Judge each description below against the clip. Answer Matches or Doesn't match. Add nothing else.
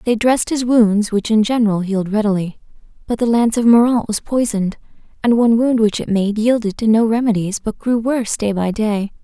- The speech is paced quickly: Matches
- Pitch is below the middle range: Doesn't match